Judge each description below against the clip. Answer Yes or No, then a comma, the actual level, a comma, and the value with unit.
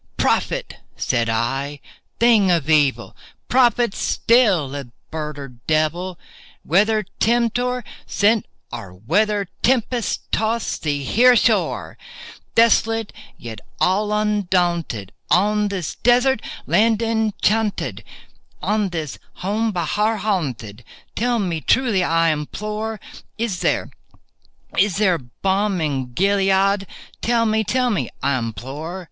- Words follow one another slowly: Yes, slow, 105 wpm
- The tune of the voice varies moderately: No, wide, 6.3 semitones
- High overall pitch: Yes, high, 195 Hz